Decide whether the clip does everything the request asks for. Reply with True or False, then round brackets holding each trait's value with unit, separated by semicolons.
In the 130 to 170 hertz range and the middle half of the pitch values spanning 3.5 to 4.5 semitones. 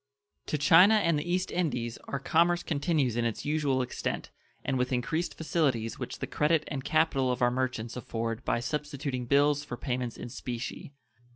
True (140 Hz; 4.2 semitones)